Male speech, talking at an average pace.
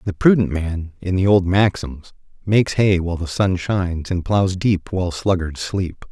Yes: male; average, 185 wpm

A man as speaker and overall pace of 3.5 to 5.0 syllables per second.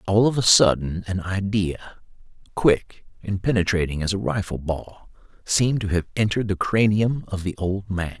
Yes: male; 4.9 syllables/s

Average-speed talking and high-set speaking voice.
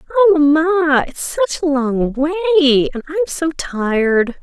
Yes: average, 165 wpm; very high, 295 Hz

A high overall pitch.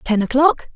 Yes: very high, 255 Hz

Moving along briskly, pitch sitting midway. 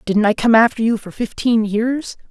No: fast, 210 wpm; high, 225 Hz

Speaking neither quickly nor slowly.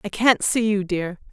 No: fast, 225 wpm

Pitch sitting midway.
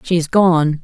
Yes: medium, 165 Hz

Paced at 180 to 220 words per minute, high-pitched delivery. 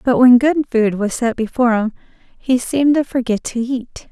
Yes: fast, 205 wpm; high, 245 Hz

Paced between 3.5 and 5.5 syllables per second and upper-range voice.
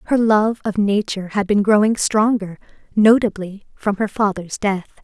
Yes: 4.8 syllables/s; high, 205 Hz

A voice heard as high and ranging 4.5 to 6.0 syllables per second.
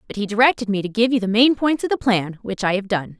No: high, 220 Hz; 6.4 syllables/s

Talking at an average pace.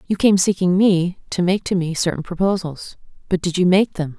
No: fast, 215 wpm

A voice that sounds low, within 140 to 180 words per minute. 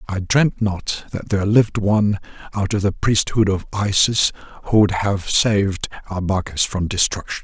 Yes: low, 100 Hz; average, 160 wpm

